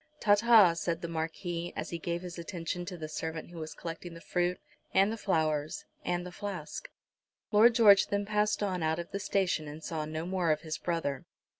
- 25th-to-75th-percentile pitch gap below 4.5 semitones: Yes, average, 3.4 semitones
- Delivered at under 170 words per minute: No, fast, 205 wpm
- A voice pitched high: No, medium, 175 Hz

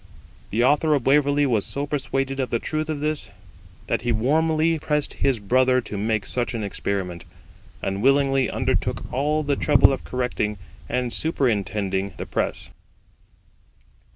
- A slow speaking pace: No, average, 150 wpm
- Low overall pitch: Yes, low, 130 Hz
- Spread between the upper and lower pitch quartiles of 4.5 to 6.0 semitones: Yes, average, 4.9 semitones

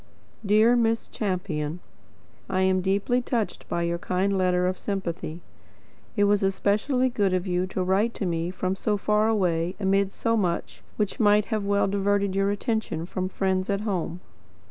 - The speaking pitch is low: No, high, 195 Hz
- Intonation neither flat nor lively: No, narrow, 2.3 semitones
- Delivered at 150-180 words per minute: Yes, average, 165 wpm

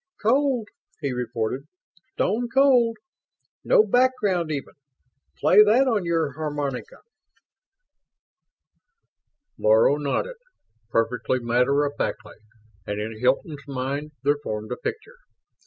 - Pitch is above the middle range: No, medium, 145 Hz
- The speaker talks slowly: Yes, slow, 105 wpm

